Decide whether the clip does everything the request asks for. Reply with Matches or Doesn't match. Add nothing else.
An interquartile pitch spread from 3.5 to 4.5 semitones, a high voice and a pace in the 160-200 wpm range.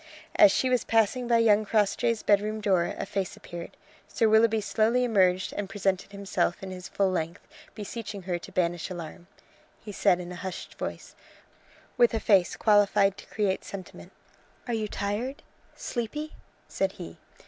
Doesn't match